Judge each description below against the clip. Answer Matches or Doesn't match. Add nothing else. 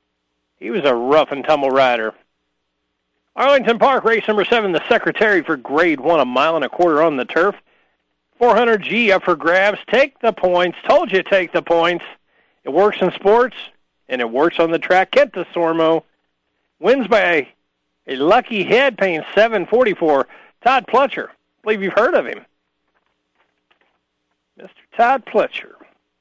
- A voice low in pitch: Doesn't match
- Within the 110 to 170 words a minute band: Matches